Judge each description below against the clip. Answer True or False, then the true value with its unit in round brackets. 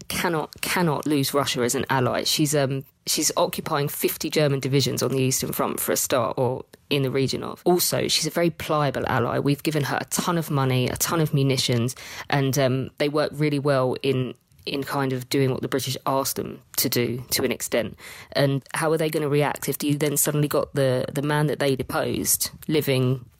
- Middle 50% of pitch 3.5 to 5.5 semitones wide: False (2.4 semitones)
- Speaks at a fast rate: True (215 wpm)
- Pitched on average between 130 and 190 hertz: True (140 Hz)